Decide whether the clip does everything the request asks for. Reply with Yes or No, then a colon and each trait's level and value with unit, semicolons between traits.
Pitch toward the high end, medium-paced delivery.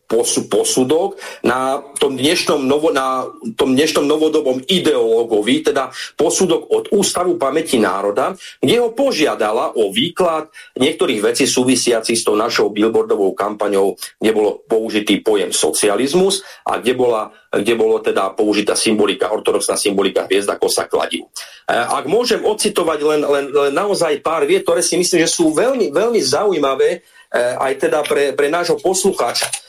Yes: high, 235 Hz; average, 145 wpm